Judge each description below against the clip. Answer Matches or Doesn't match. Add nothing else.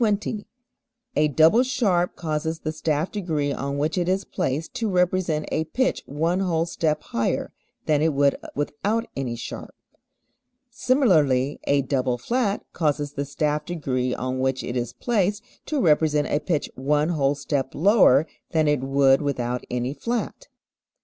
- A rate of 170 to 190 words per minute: Doesn't match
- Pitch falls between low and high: Matches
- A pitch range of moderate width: Matches